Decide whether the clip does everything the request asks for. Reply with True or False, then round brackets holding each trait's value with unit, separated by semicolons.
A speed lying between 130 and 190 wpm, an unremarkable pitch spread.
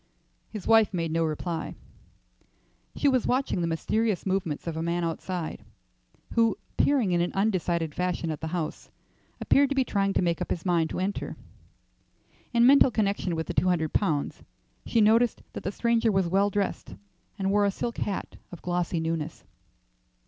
True (175 wpm; 4.6 semitones)